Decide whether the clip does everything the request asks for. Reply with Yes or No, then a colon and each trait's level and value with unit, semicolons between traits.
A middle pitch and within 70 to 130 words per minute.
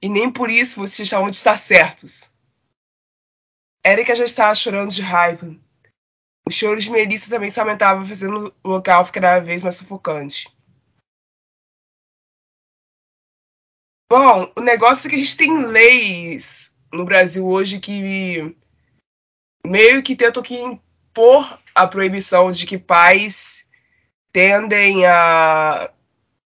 No: high, 195 Hz; slow, 120 wpm